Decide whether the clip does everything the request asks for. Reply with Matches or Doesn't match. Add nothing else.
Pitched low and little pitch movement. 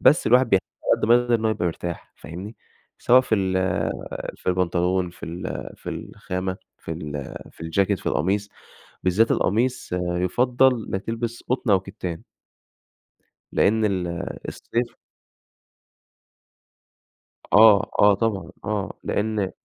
Doesn't match